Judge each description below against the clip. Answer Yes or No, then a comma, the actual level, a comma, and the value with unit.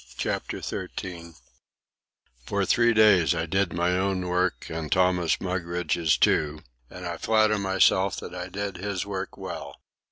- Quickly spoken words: No, average, 140 wpm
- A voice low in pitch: Yes, very low, 90 Hz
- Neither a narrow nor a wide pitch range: No, narrow, 2.3 semitones